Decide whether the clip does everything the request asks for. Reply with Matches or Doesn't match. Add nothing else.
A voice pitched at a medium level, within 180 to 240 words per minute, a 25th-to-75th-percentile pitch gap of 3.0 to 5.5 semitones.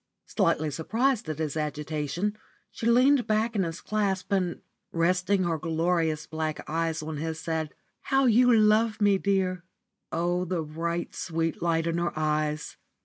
Doesn't match